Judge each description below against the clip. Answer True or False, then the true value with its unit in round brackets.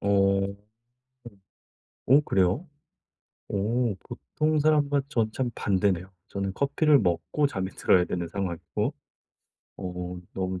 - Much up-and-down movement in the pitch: True (7.0 semitones)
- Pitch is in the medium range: False (100 Hz)